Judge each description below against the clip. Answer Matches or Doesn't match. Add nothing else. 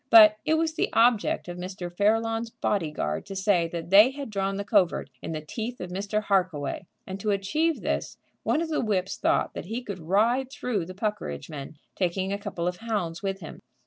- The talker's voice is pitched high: Matches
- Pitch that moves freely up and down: Doesn't match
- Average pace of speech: Doesn't match